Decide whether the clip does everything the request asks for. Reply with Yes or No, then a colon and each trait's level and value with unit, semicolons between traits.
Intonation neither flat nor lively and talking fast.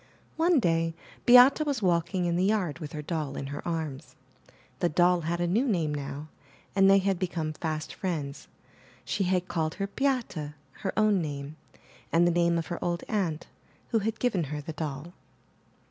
No: average, 4.0 semitones; average, 180 wpm